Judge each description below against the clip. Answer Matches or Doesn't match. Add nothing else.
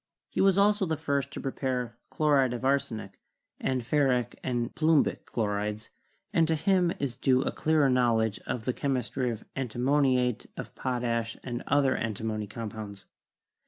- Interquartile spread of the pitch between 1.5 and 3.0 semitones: Doesn't match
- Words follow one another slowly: Doesn't match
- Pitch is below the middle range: Matches